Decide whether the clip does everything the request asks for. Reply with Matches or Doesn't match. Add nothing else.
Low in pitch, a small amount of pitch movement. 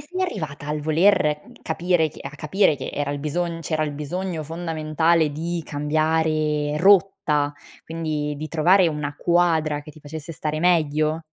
Doesn't match